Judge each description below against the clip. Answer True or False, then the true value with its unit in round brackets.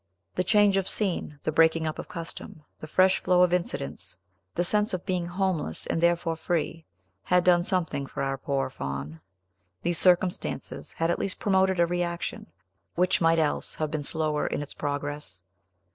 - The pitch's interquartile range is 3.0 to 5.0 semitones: True (3.3 semitones)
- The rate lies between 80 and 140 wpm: False (175 wpm)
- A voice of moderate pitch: True (170 Hz)